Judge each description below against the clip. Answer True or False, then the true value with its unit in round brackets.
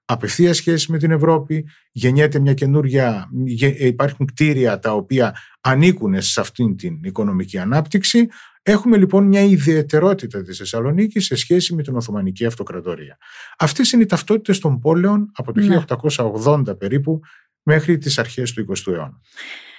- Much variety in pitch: True (6.2 semitones)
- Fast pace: False (140 wpm)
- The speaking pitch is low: False (150 Hz)